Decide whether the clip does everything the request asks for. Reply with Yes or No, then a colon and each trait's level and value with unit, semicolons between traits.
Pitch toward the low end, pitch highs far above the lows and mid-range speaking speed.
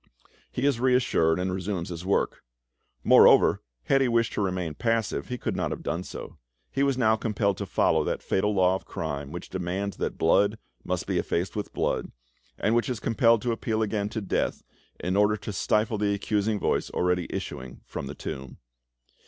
No: low, 100 Hz; average, 3.7 semitones; average, 190 wpm